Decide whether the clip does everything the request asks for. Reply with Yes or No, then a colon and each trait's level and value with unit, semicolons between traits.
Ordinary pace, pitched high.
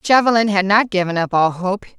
No: fast, 210 wpm; high, 200 Hz